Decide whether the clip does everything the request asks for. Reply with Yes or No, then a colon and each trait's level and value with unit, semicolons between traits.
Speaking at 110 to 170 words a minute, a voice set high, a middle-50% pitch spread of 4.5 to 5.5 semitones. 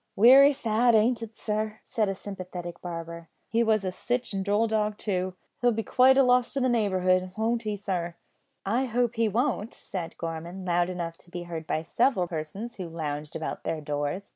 No: average, 190 wpm; high, 200 Hz; average, 4.9 semitones